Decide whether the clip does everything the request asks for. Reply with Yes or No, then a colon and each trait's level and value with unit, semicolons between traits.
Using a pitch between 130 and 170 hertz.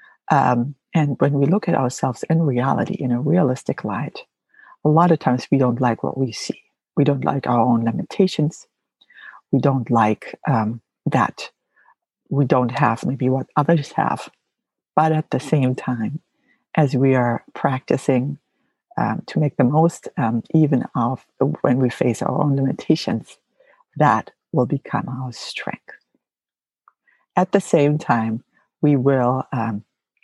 Yes: low, 135 Hz